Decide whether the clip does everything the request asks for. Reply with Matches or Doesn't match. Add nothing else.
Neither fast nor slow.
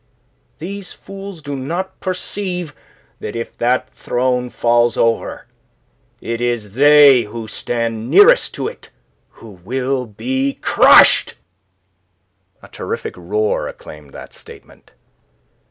Doesn't match